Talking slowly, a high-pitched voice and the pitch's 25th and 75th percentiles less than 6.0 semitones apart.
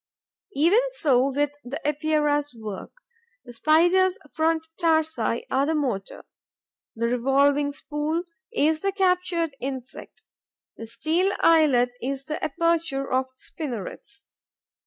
Yes: slow, 115 wpm; very high, 295 Hz; average, 3.8 semitones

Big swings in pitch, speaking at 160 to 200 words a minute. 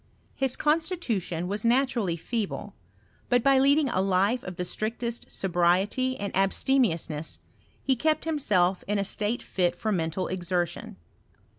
No: wide, 6.3 semitones; average, 145 wpm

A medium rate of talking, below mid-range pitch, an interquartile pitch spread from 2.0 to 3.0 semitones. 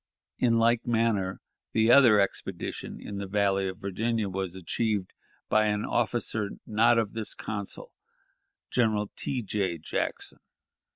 No: slow, 130 wpm; low, 105 Hz; average, 2.7 semitones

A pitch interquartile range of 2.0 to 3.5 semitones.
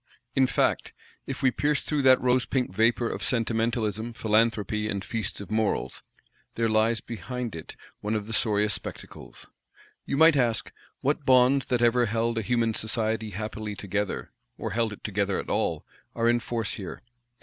Yes: narrow, 2.5 semitones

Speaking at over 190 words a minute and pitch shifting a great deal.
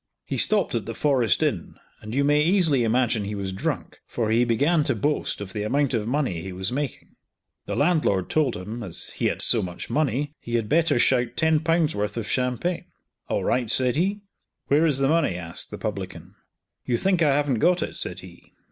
Yes: fast, 205 wpm; wide, 6.0 semitones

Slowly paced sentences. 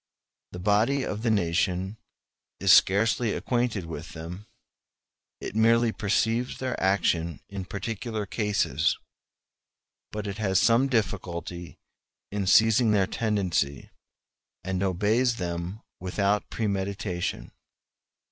Yes: slow, 105 wpm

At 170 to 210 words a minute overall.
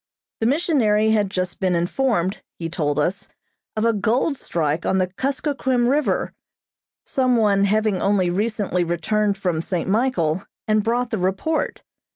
No: average, 150 wpm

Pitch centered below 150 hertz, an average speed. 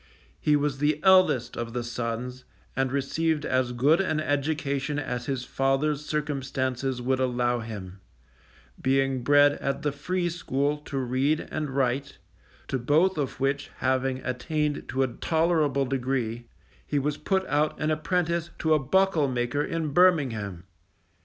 Yes: medium, 140 Hz; average, 145 wpm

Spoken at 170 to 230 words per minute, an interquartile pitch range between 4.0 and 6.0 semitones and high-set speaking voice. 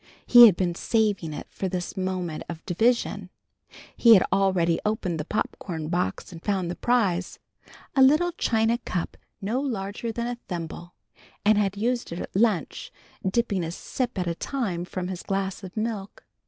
Yes: average, 175 wpm; average, 4.5 semitones; high, 195 Hz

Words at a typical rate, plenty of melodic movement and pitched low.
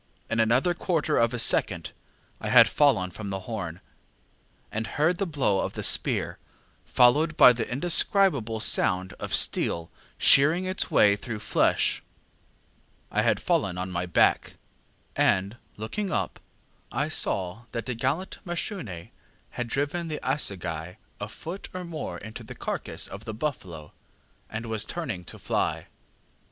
Yes: average, 145 wpm; wide, 8.0 semitones; low, 115 Hz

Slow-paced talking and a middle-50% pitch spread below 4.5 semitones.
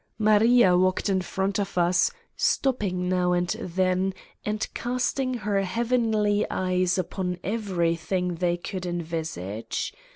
Yes: slow, 120 wpm; average, 2.9 semitones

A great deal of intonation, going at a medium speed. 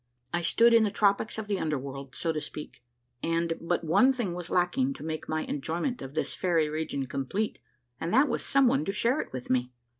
No: wide, 6.3 semitones; fast, 220 wpm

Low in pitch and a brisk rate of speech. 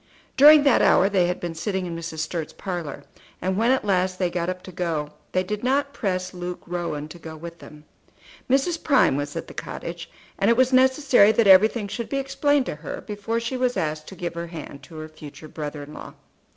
No: medium, 185 Hz; fast, 220 wpm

